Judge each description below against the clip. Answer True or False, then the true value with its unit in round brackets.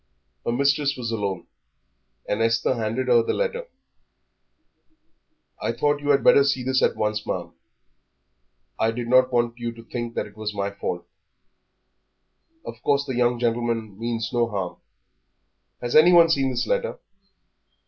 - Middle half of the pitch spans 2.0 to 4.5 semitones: True (3.4 semitones)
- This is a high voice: False (120 Hz)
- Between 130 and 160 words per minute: True (150 wpm)